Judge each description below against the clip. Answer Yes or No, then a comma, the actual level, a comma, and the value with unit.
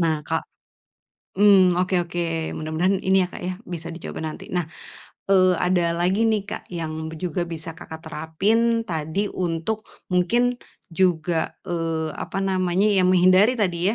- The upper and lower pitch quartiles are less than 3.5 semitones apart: Yes, average, 2.8 semitones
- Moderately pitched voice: Yes, medium, 180 Hz